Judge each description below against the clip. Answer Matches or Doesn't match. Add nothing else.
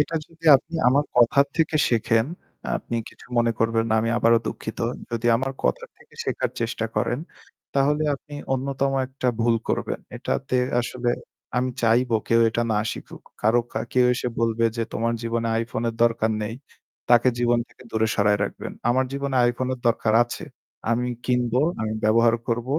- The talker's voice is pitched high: Doesn't match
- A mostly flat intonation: Matches